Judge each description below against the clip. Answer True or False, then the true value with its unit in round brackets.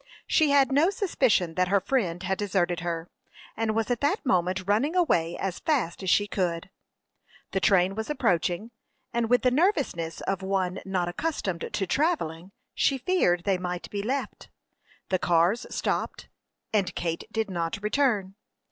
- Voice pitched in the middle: False (195 Hz)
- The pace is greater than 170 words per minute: False (160 wpm)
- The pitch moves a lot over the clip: True (6.0 semitones)